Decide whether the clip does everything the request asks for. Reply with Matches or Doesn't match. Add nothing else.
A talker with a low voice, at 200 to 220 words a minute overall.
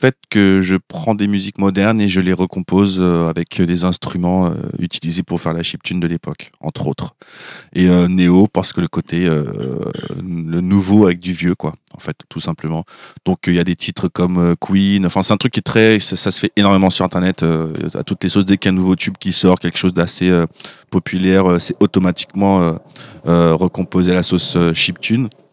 Matches